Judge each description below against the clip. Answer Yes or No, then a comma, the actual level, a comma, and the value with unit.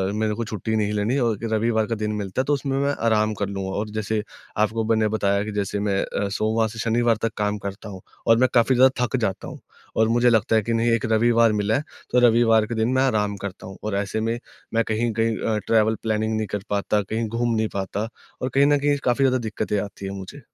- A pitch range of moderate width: No, narrow, 2.1 semitones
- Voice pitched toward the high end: No, low, 110 Hz